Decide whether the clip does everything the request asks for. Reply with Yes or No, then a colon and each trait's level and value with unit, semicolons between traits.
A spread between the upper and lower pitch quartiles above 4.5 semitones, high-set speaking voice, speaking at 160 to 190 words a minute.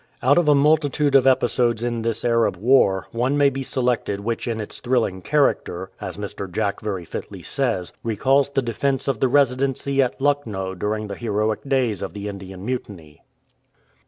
No: average, 4.9 semitones; low, 120 Hz; average, 175 wpm